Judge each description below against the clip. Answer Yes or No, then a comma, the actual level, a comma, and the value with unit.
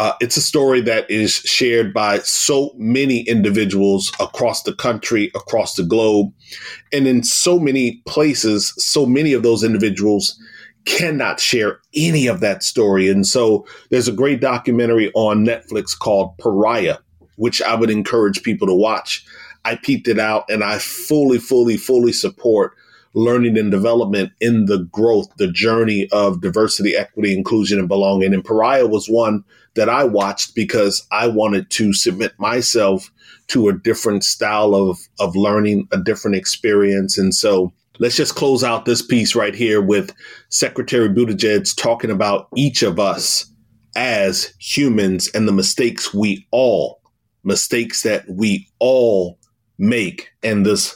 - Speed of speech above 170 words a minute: No, average, 150 wpm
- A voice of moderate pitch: No, low, 110 Hz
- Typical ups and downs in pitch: Yes, average, 3.0 semitones